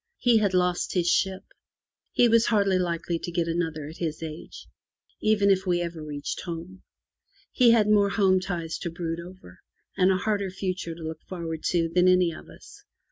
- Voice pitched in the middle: Yes, medium, 180 Hz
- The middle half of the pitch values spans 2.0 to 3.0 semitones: Yes, narrow, 2.6 semitones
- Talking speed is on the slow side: No, average, 190 wpm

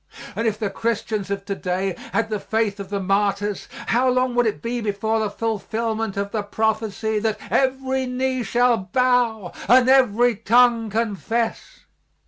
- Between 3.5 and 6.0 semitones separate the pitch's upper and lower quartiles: No, average, 3.1 semitones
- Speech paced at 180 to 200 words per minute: No, average, 160 wpm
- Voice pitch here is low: No, high, 225 Hz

